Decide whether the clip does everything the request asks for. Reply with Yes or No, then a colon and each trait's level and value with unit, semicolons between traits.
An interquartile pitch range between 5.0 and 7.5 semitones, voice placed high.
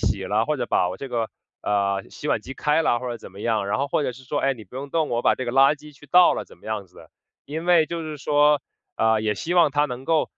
No: average, 5.3 semitones; low, 135 Hz